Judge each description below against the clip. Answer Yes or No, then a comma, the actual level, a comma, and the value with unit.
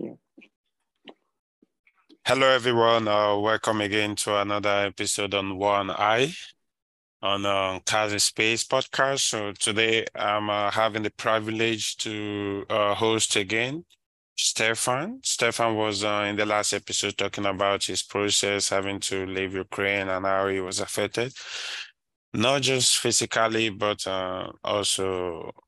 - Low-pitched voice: Yes, low, 105 Hz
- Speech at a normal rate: No, slow, 125 wpm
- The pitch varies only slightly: Yes, narrow, 2.0 semitones